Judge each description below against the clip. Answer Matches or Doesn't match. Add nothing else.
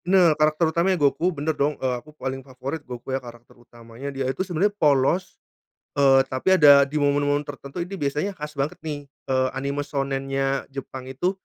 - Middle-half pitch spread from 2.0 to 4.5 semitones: Matches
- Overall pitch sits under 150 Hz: Matches